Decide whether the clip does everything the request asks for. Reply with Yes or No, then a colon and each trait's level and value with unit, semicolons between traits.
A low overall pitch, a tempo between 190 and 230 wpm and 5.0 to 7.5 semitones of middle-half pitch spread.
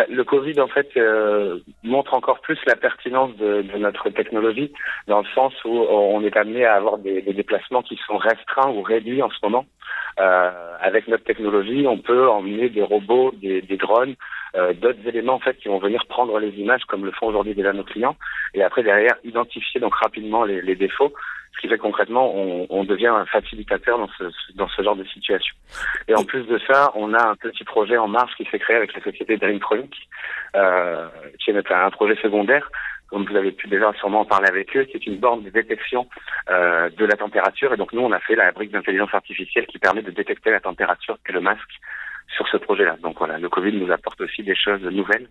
Yes: low, 115 Hz; fast, 220 wpm; wide, 5.6 semitones